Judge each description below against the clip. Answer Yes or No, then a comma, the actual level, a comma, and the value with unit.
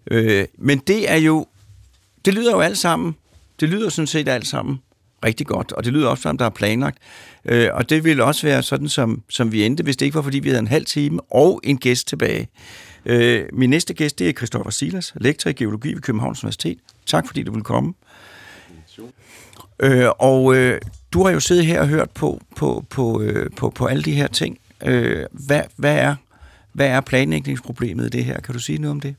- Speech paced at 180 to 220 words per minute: Yes, average, 205 wpm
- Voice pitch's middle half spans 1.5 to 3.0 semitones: No, average, 4.9 semitones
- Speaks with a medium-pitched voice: No, low, 130 Hz